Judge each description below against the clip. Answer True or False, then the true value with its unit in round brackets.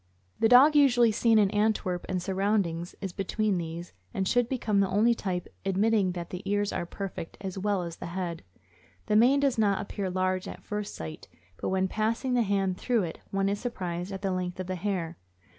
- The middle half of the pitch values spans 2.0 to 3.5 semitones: True (3.0 semitones)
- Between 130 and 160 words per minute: False (205 wpm)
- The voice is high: True (195 Hz)